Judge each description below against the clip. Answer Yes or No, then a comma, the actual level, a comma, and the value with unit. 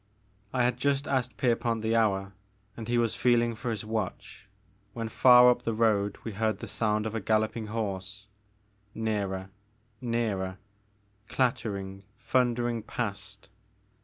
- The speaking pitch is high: No, low, 110 Hz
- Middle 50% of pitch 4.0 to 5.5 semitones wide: No, average, 2.7 semitones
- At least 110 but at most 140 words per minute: Yes, slow, 135 wpm